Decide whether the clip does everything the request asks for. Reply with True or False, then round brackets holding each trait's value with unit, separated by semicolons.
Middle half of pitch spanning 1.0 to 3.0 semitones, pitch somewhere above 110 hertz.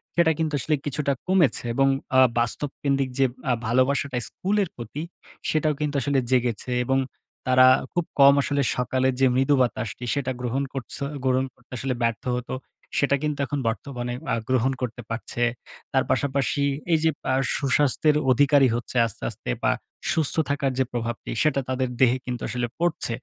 True (2.5 semitones; 135 Hz)